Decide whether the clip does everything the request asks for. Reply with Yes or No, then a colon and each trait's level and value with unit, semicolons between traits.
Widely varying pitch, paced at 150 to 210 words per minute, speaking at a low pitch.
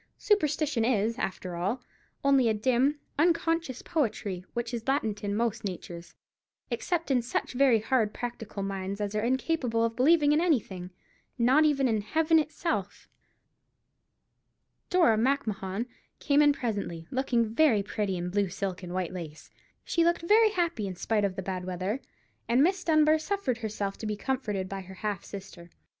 No: wide, 6.6 semitones; average, 160 wpm; high, 230 Hz